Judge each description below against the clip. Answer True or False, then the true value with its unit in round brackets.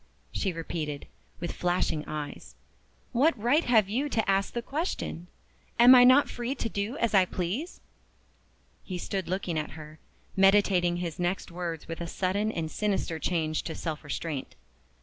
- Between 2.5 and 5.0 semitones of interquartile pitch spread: False (5.5 semitones)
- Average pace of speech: True (160 wpm)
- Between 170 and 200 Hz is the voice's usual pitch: True (185 Hz)